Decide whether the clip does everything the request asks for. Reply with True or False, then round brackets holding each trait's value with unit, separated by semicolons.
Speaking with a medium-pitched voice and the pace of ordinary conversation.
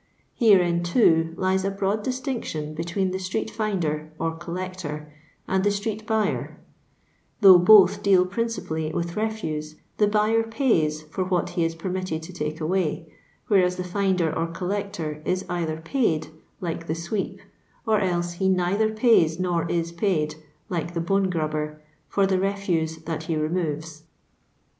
True (180 Hz; 150 wpm)